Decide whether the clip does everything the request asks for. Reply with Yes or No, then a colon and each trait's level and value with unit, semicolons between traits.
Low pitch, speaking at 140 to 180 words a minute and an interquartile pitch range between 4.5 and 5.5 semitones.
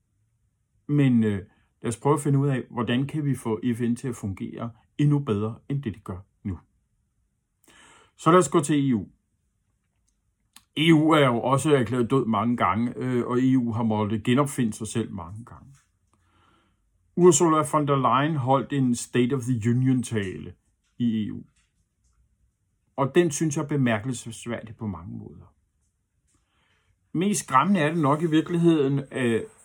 Yes: low, 120 Hz; average, 160 wpm; average, 4.8 semitones